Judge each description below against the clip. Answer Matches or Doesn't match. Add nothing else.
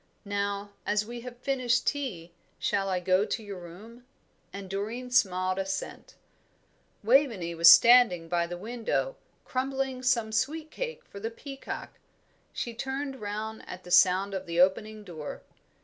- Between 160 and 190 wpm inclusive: Doesn't match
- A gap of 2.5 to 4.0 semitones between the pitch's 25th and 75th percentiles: Doesn't match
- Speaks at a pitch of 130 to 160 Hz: Doesn't match